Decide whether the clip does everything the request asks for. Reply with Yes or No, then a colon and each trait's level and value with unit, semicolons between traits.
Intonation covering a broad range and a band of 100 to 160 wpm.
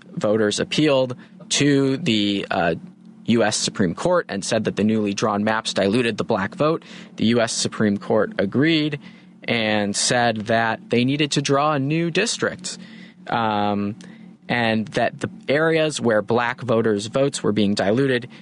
Yes: wide, 6.9 semitones; average, 150 wpm